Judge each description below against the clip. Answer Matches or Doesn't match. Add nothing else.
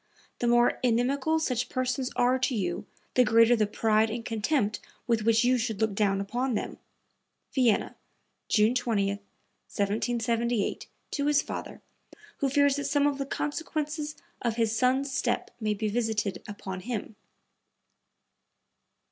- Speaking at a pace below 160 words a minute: Matches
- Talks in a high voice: Matches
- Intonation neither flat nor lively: Matches